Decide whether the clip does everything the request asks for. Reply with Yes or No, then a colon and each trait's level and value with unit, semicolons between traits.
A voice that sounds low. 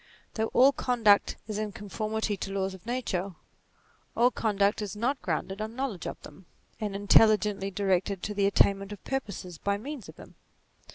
No: high, 205 Hz